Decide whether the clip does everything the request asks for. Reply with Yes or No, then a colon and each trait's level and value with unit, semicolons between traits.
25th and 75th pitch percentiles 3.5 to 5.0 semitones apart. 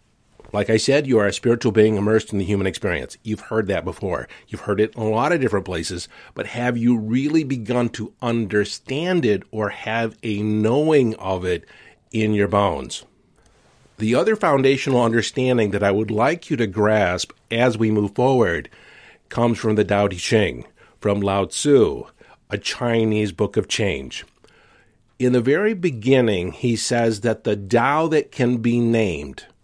No: average, 3.0 semitones